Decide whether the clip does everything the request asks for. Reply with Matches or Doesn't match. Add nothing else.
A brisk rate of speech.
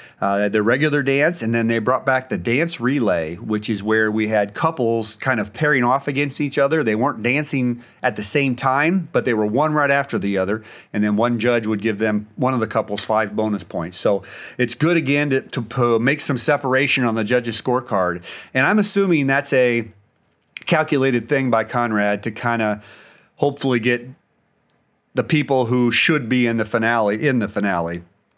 Doesn't match